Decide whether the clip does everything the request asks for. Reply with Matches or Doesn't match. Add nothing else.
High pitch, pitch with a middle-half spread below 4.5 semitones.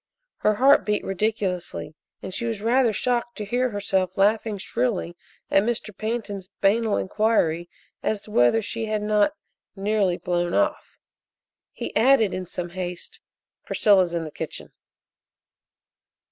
Matches